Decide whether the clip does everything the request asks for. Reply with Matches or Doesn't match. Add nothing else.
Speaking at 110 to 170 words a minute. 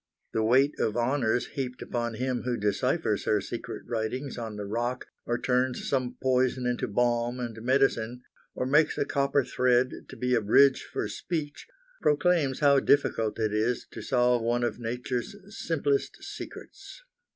Matches